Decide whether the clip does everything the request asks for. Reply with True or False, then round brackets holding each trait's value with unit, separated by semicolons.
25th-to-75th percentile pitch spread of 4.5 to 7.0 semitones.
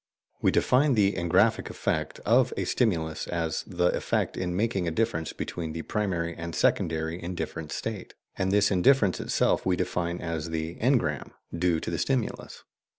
False (3.8 semitones)